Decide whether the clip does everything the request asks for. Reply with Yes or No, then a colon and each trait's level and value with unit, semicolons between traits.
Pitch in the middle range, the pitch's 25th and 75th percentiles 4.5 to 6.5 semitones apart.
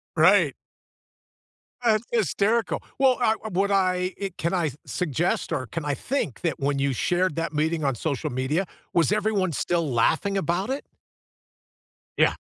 Yes: medium, 175 Hz; average, 5.2 semitones